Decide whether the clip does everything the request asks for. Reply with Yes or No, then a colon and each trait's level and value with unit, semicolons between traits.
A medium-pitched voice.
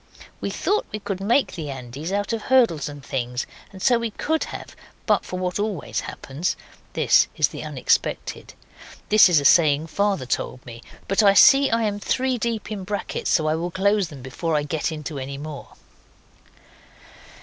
Yes: medium, 180 Hz